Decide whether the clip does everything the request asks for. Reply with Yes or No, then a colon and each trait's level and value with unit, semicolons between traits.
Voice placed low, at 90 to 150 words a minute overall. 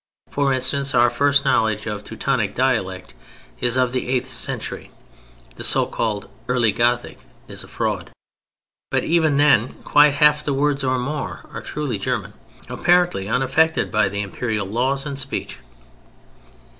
Yes: low, 130 Hz; average, 145 wpm